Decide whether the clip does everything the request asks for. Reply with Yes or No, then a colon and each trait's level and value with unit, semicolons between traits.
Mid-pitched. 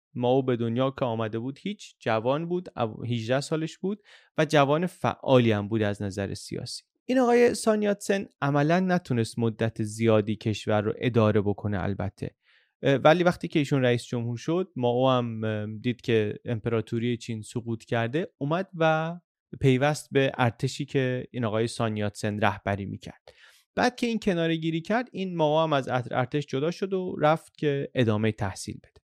No: low, 130 Hz